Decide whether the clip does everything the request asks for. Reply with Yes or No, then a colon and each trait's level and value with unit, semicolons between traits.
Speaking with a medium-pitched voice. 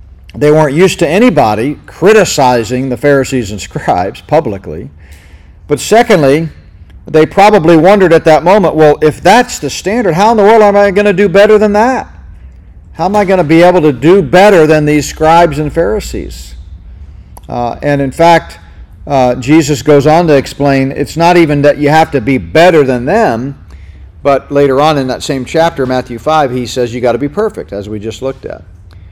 Yes: medium, 145 Hz